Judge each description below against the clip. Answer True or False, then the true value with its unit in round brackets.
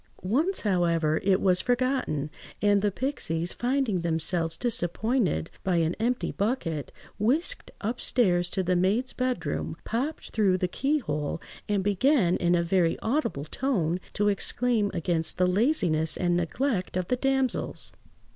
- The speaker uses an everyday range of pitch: False (6.3 semitones)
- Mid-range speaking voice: False (195 Hz)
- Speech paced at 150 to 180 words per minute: False (135 wpm)